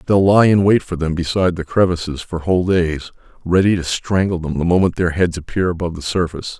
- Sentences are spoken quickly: Yes, fast, 220 wpm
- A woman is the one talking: No, male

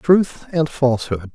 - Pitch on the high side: No, medium, 140 Hz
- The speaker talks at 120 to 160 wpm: Yes, slow, 135 wpm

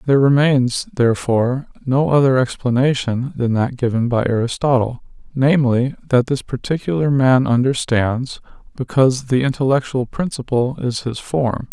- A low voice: Yes, low, 130 Hz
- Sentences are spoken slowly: Yes, slow, 120 wpm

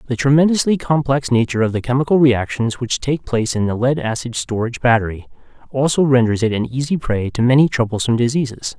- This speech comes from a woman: No, male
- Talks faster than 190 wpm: No, average, 185 wpm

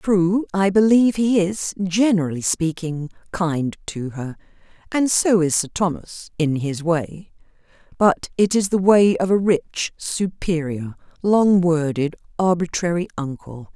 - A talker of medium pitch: Yes, medium, 175 Hz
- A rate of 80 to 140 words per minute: Yes, slow, 135 wpm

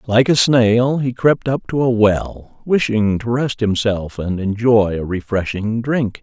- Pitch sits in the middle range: No, low, 115 Hz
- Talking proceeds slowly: No, average, 175 wpm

